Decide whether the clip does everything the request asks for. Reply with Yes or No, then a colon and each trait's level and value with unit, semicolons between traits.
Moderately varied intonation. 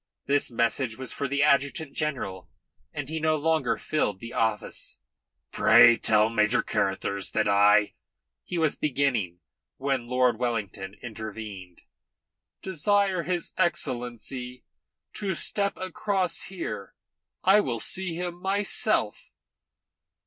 No: wide, 7.2 semitones